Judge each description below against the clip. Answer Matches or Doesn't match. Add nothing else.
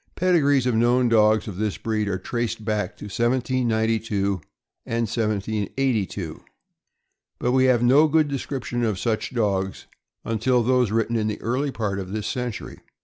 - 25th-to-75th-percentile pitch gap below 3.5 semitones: Matches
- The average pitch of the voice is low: Matches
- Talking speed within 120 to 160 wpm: Matches